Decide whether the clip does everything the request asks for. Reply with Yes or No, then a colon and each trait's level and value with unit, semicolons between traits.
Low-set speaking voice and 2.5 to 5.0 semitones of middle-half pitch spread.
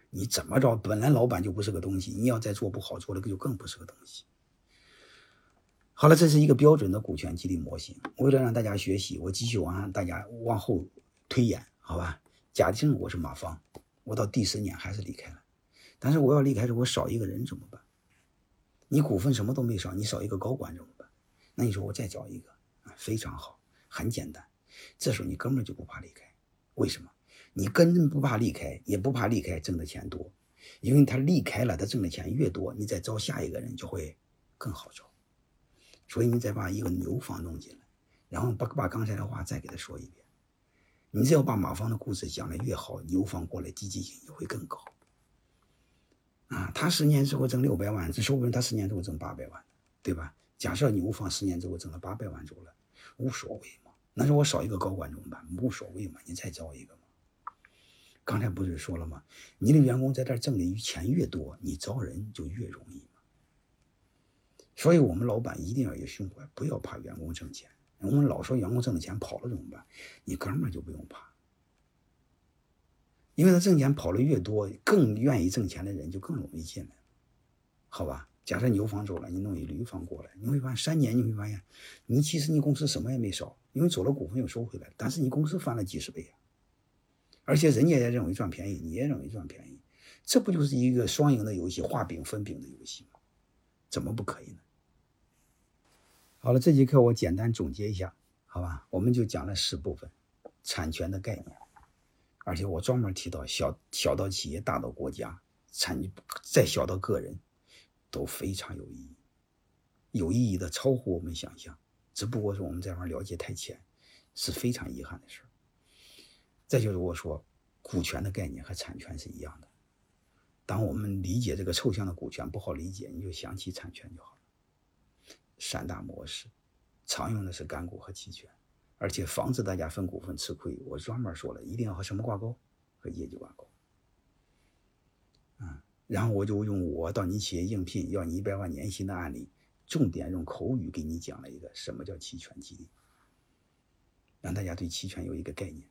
No: low, 105 Hz; wide, 5.5 semitones